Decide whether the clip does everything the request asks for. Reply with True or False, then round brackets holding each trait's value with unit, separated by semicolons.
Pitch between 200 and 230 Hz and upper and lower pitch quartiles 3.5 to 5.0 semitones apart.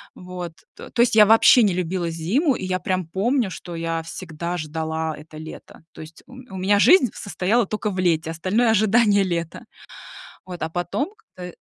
False (185 Hz; 4.5 semitones)